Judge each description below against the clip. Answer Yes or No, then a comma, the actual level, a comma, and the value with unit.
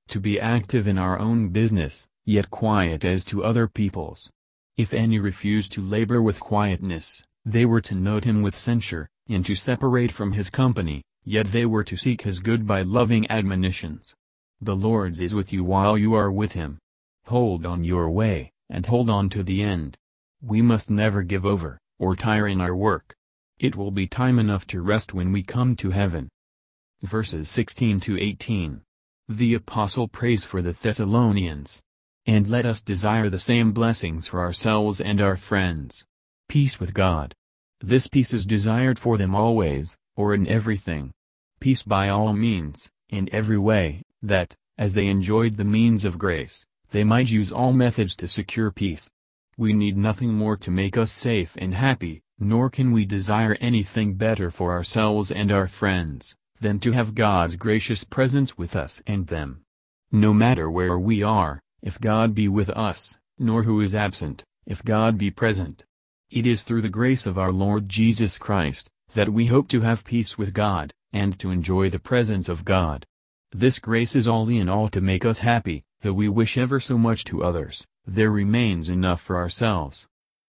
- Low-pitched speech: Yes, low, 105 Hz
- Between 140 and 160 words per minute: No, average, 180 wpm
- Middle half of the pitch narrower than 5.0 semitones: Yes, average, 3.5 semitones